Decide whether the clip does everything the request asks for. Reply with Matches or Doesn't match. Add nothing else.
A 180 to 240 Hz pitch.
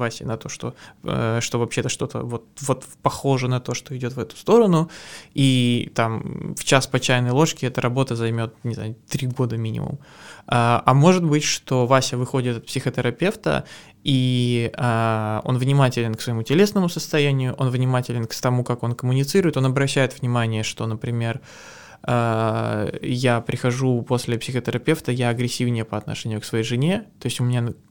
Doesn't match